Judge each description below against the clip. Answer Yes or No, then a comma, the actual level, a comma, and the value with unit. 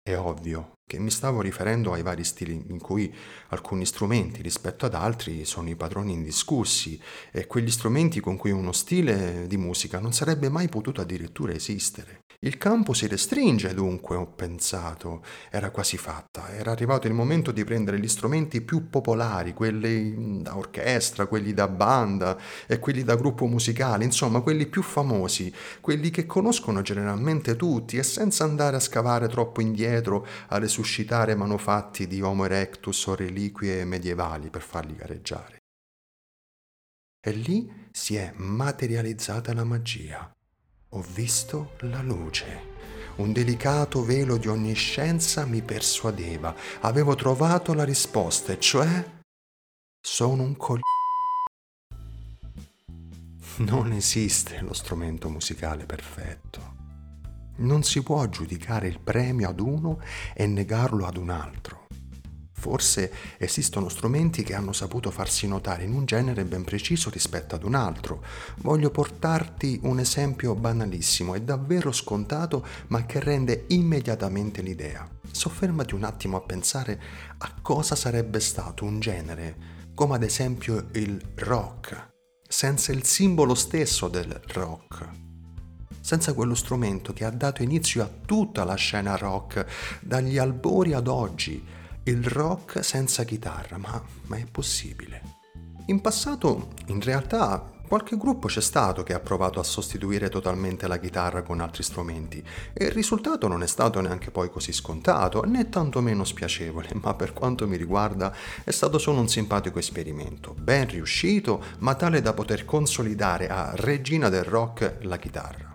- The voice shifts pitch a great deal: Yes, wide, 5.9 semitones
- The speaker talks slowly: No, average, 140 wpm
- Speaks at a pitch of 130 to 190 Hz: No, low, 110 Hz